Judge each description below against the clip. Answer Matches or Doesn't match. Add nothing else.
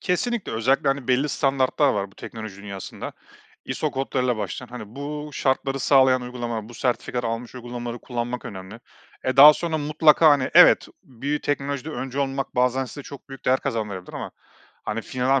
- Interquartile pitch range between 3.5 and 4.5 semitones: Doesn't match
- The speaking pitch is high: Doesn't match